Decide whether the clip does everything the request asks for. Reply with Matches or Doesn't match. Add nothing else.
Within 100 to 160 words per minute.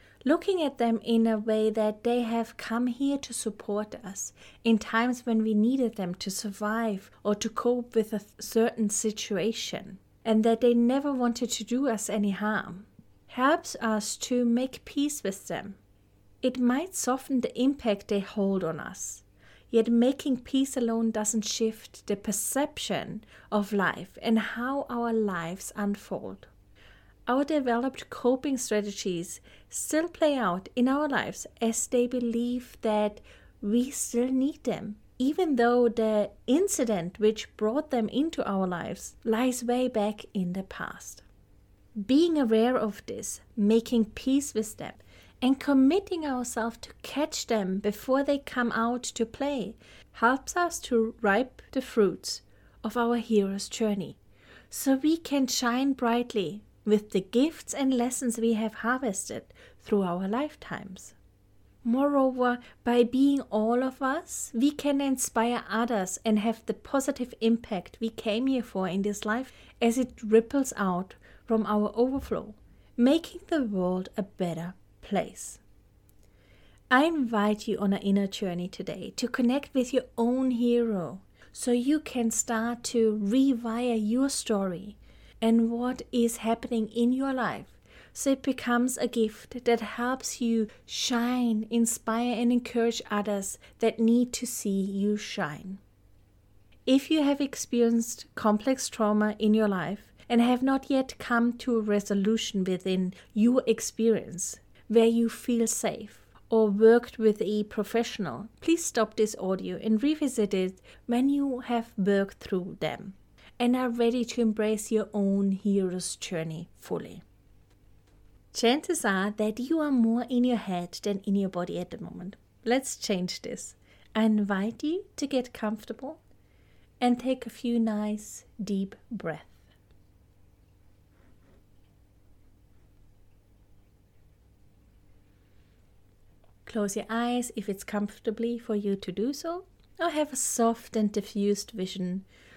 Matches